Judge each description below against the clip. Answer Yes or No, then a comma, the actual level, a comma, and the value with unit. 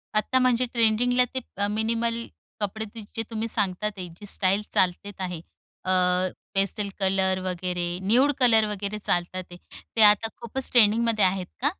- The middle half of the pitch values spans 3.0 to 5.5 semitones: Yes, average, 3.5 semitones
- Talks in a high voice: Yes, high, 210 Hz